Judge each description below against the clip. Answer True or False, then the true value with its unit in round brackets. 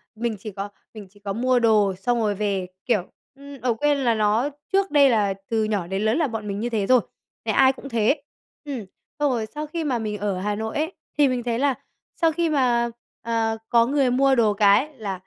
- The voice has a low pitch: False (230 Hz)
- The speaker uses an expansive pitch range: False (4.5 semitones)